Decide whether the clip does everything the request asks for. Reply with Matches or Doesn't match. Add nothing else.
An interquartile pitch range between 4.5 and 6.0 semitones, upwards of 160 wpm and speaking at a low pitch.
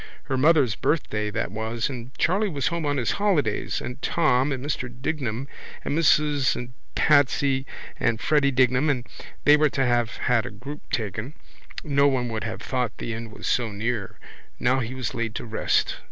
Doesn't match